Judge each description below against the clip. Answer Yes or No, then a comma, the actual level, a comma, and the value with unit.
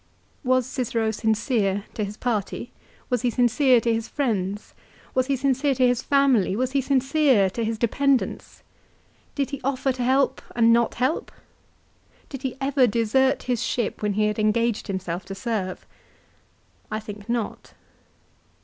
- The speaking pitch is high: Yes, high, 240 Hz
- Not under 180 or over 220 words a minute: No, average, 155 wpm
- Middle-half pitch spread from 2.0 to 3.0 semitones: No, average, 3.6 semitones